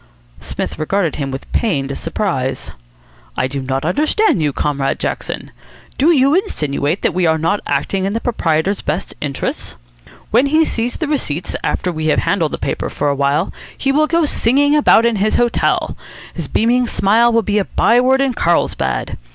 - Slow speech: No, average, 175 wpm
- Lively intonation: Yes, wide, 8.6 semitones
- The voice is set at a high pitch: Yes, high, 200 Hz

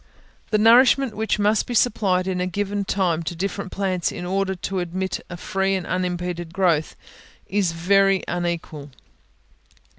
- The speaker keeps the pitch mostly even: Yes, narrow, 2.2 semitones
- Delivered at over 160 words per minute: No, average, 150 wpm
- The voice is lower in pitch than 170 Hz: No, high, 190 Hz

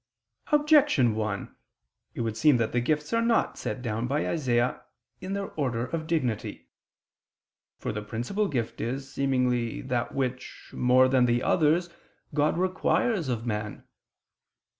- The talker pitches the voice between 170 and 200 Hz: No, low, 130 Hz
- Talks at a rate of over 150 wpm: No, average, 140 wpm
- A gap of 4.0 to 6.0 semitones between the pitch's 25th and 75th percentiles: Yes, average, 5.2 semitones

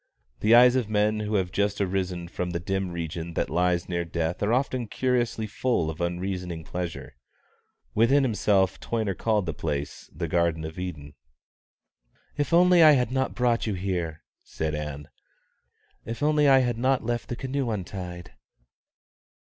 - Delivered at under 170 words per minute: Yes, average, 160 wpm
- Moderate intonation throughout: No, wide, 5.7 semitones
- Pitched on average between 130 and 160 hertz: No, very low, 95 Hz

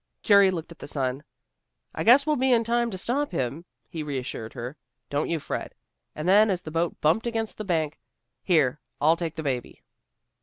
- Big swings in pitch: Yes, wide, 6.8 semitones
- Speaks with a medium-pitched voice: Yes, medium, 165 Hz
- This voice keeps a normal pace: Yes, average, 195 wpm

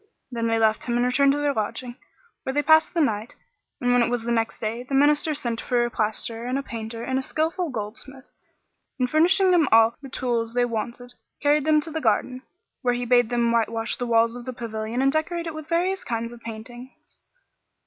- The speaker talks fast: Yes, fast, 220 wpm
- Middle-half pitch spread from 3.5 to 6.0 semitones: Yes, average, 4.0 semitones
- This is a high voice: Yes, high, 245 Hz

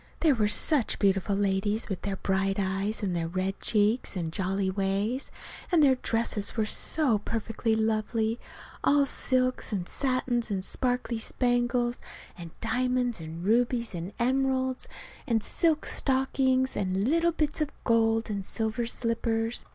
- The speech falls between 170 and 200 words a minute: No, average, 145 wpm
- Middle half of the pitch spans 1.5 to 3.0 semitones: No, average, 4.3 semitones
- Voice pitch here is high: Yes, high, 225 Hz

